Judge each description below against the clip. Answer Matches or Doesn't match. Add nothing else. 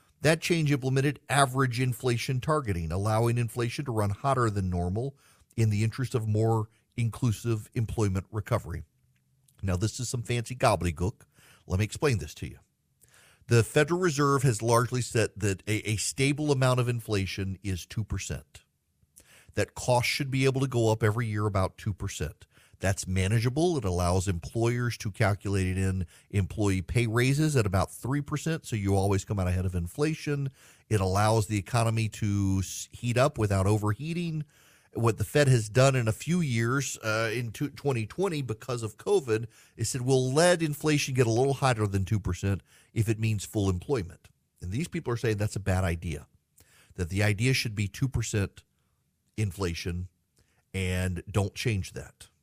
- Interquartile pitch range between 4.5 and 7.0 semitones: Matches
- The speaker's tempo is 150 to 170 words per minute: Matches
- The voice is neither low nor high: Doesn't match